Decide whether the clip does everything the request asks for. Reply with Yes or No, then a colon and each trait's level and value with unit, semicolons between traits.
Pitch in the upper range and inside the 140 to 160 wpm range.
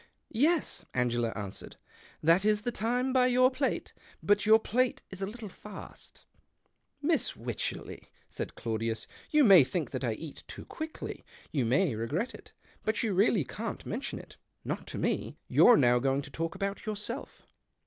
No: high, 200 Hz; average, 180 wpm